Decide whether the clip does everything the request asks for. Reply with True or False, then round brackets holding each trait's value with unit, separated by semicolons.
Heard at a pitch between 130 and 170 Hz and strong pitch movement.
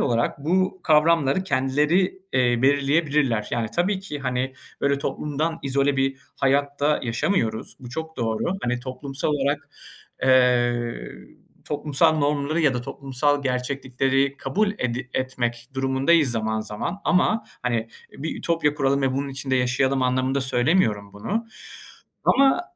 False (135 Hz; 3.1 semitones)